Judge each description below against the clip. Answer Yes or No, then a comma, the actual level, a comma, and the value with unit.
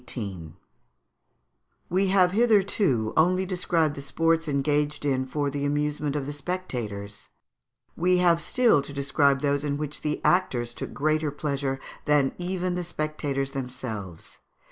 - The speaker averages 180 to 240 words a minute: No, average, 140 wpm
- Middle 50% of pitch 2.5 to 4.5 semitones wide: Yes, average, 4.2 semitones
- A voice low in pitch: No, medium, 150 Hz